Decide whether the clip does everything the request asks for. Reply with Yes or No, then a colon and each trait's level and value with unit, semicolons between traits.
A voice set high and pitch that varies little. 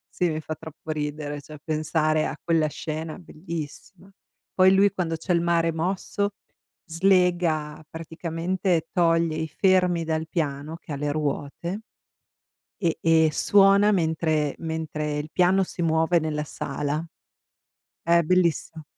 No: medium, 160 Hz; narrow, 2.3 semitones